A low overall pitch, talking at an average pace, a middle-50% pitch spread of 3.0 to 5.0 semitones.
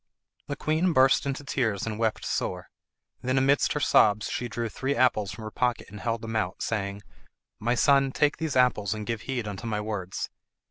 Yes: low, 115 Hz; average, 195 wpm; average, 3.9 semitones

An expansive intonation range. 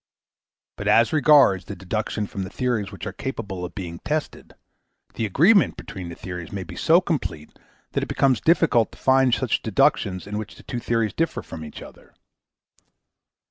Yes: wide, 6.2 semitones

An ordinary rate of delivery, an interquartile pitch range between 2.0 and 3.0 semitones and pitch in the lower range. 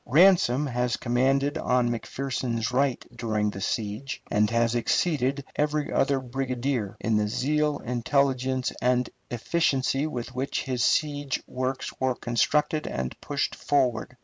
No: slow, 130 wpm; average, 2.7 semitones; low, 130 Hz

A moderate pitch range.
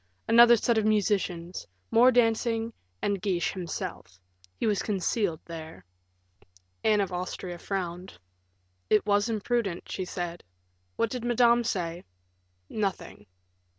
Yes: average, 4.3 semitones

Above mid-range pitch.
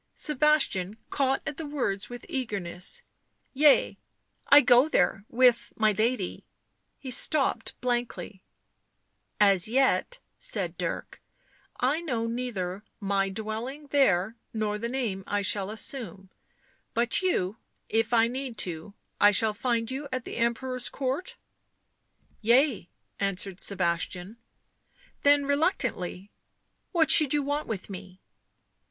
Yes: high, 235 Hz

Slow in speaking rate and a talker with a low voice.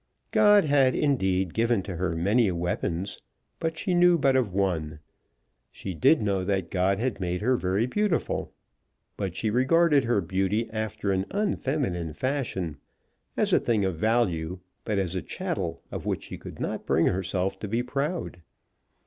No: average, 165 wpm; low, 100 Hz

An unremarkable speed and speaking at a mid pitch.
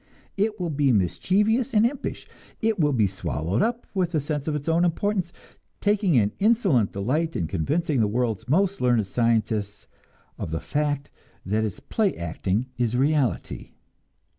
Yes: average, 160 wpm; medium, 145 Hz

